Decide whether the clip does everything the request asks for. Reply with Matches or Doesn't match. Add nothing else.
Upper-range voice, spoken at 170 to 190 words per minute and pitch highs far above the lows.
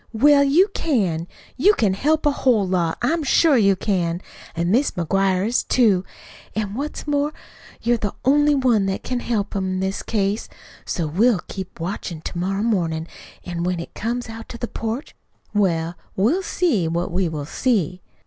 Matches